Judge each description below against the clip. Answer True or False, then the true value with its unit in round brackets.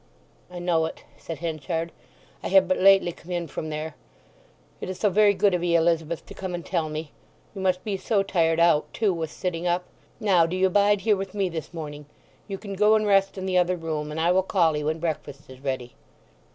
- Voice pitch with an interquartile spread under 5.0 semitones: True (3.1 semitones)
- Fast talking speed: True (230 wpm)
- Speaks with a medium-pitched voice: True (175 Hz)